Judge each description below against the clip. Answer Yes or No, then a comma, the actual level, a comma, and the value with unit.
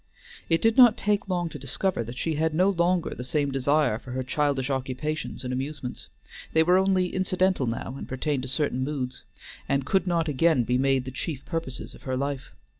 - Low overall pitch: No, medium, 145 Hz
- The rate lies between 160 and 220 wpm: Yes, average, 200 wpm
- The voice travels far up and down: No, average, 4.9 semitones